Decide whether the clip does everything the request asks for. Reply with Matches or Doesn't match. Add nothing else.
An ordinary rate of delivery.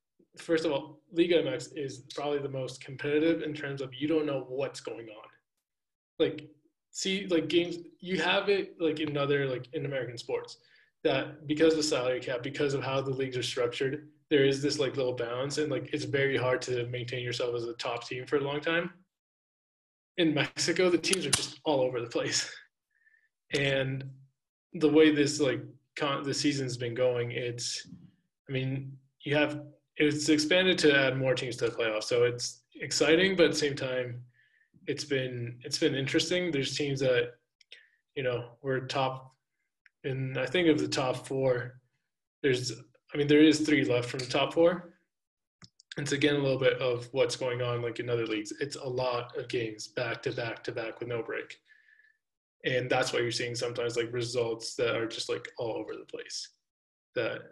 Matches